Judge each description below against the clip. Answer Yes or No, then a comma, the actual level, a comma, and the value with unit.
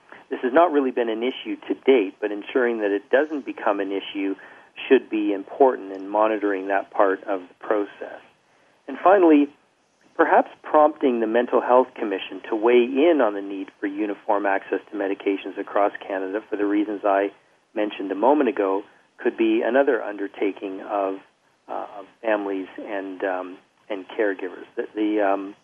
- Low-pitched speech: Yes, low, 105 Hz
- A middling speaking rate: Yes, average, 170 wpm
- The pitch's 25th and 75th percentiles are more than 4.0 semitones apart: Yes, average, 4.7 semitones